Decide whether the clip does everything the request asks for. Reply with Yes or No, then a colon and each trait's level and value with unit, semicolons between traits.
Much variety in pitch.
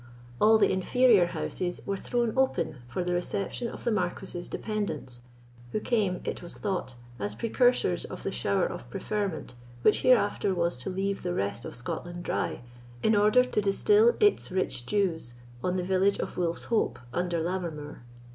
No: average, 3.8 semitones